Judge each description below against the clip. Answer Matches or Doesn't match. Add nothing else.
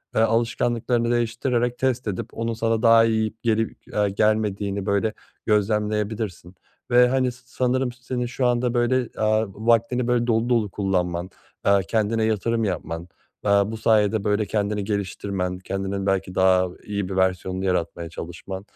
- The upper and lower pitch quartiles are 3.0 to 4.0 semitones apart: Matches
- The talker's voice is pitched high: Doesn't match